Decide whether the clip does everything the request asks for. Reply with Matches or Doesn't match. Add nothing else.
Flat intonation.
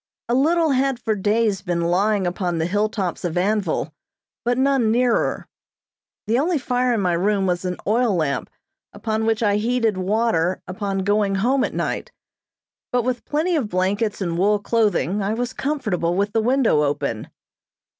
Doesn't match